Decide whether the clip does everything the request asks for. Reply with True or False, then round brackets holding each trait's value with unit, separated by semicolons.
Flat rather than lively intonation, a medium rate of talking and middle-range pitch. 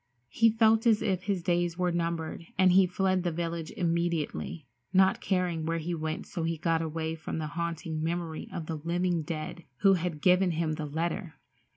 True (2.1 semitones; 190 wpm; 170 Hz)